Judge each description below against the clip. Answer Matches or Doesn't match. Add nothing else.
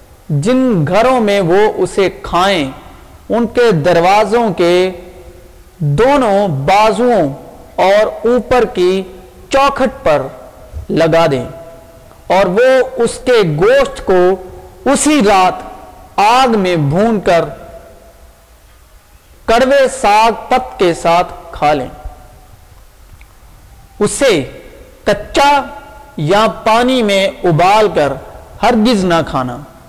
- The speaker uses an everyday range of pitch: Doesn't match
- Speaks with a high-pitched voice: Matches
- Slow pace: Matches